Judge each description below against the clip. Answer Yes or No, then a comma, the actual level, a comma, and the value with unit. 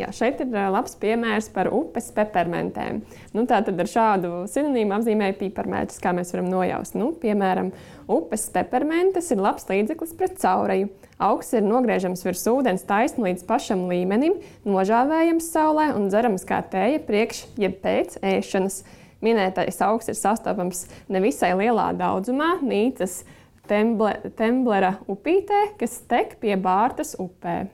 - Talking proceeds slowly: Yes, slow, 130 wpm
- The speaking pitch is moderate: No, high, 215 Hz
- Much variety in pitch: No, average, 4.7 semitones